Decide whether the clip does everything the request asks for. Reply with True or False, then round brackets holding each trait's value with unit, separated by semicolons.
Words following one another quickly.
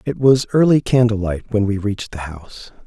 True (210 wpm)